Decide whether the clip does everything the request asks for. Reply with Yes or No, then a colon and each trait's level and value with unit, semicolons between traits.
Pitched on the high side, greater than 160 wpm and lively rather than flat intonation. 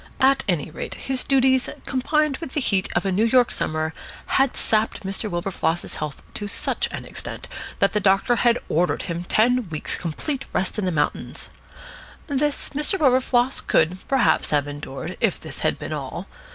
Yes: high, 215 Hz; average, 175 wpm; wide, 7.1 semitones